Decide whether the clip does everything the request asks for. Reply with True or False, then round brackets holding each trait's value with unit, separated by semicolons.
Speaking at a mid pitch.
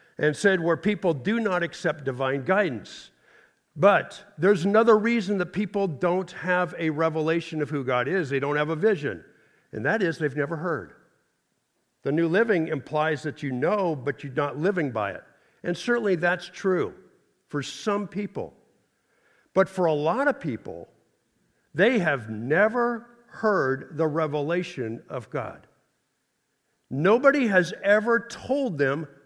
True (170 Hz)